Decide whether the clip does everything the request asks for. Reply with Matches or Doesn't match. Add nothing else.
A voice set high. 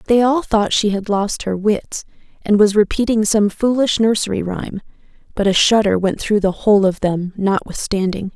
Matches